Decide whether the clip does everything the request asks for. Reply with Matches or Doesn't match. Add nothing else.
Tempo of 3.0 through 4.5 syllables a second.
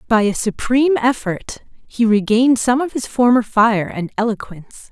Doesn't match